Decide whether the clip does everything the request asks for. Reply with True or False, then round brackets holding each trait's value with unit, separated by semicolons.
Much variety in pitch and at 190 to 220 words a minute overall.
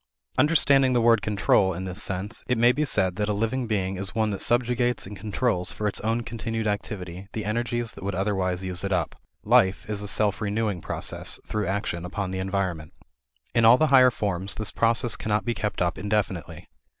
False (3.3 semitones; 200 wpm)